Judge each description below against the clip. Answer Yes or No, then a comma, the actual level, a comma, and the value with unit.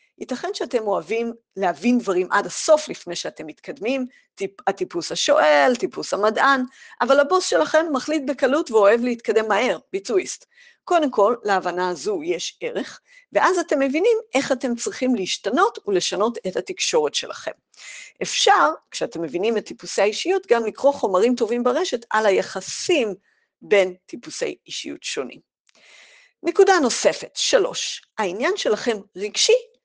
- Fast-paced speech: No, average, 130 wpm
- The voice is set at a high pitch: Yes, very high, 265 Hz